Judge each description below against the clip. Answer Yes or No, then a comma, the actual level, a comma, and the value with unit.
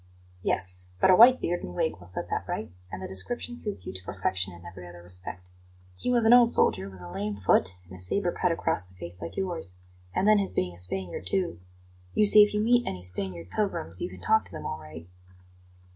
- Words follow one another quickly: Yes, fast, 235 wpm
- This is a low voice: Yes, very low, 95 Hz